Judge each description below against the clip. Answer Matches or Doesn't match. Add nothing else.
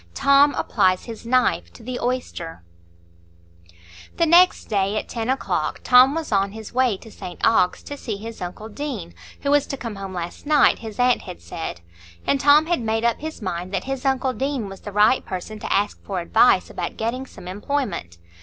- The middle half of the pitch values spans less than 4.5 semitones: Doesn't match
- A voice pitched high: Matches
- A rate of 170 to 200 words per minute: Matches